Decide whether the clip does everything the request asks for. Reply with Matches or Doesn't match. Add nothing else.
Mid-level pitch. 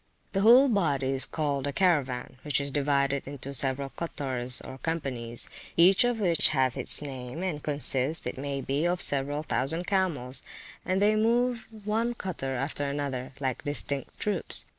Matches